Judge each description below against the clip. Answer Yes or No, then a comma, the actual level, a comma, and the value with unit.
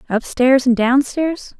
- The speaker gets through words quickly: No, slow, 115 wpm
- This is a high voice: Yes, very high, 265 Hz